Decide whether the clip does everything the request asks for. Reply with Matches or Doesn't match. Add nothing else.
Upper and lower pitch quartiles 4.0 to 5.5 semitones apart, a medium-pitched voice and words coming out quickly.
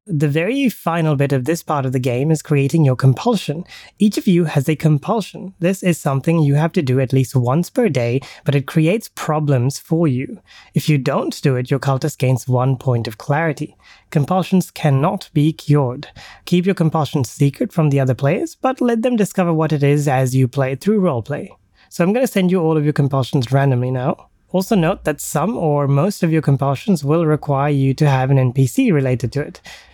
Matches